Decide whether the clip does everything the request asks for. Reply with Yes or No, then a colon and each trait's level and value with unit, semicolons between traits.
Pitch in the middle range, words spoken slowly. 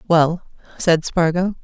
Yes: medium, 170 Hz; slow, 110 wpm